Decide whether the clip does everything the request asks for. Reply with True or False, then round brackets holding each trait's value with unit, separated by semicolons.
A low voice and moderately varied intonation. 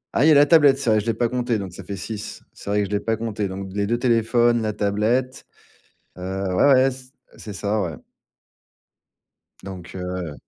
True (105 Hz; 3.7 semitones)